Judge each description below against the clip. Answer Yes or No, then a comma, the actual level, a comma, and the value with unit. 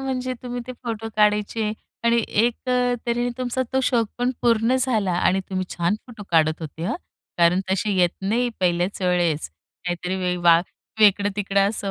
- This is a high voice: Yes, high, 205 Hz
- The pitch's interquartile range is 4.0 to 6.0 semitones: Yes, average, 5.1 semitones